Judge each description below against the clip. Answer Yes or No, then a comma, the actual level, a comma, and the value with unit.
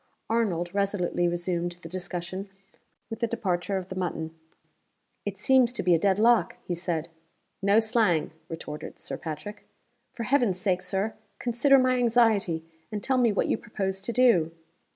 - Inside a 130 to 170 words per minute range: Yes, average, 160 wpm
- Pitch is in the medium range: No, high, 195 Hz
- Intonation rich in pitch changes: No, average, 4.7 semitones